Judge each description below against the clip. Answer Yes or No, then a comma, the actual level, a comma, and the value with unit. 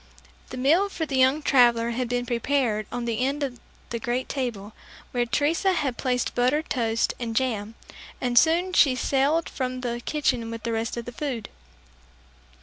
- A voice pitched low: No, very high, 250 Hz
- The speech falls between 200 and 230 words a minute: No, average, 175 wpm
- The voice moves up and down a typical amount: Yes, average, 3.1 semitones